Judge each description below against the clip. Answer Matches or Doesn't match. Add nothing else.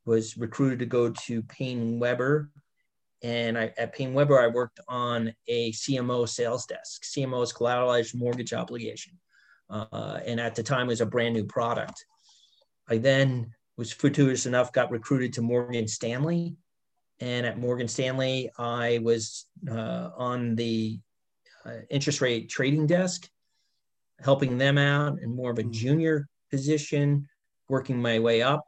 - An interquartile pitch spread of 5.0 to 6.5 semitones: Doesn't match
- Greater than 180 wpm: Doesn't match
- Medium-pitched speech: Doesn't match